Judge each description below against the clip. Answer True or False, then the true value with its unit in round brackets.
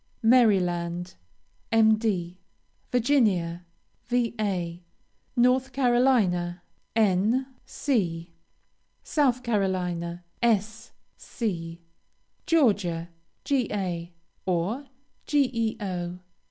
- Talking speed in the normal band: False (60 wpm)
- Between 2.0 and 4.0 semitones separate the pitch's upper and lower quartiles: False (5.6 semitones)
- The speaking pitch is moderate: False (205 Hz)